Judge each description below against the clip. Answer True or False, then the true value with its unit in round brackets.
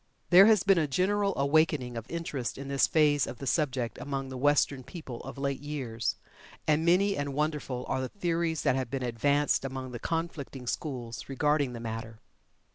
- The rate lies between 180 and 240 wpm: True (185 wpm)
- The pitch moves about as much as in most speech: True (3.8 semitones)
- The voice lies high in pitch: False (140 Hz)